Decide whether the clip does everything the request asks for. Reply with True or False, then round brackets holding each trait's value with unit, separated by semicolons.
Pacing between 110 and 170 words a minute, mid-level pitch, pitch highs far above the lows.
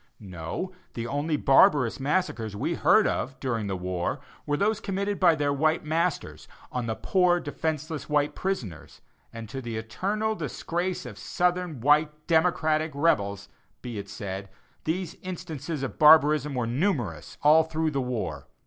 True (150 wpm; 150 Hz; 6.1 semitones)